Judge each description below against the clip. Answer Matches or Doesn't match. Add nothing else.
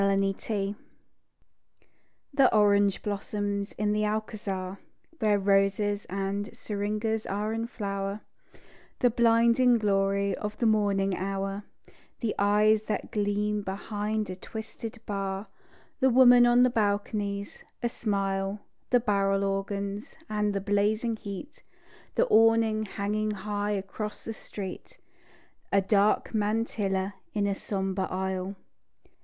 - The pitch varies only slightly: Matches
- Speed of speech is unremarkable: Doesn't match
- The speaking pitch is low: Doesn't match